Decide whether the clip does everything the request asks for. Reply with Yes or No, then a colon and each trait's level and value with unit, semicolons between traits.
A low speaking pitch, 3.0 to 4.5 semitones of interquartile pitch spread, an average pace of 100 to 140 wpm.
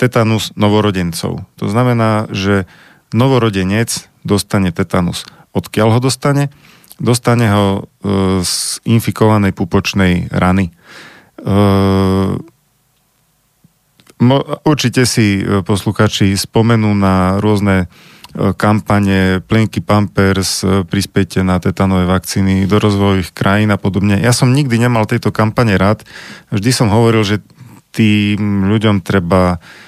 Yes: low, 105 Hz; average, 3.3 semitones; slow, 110 wpm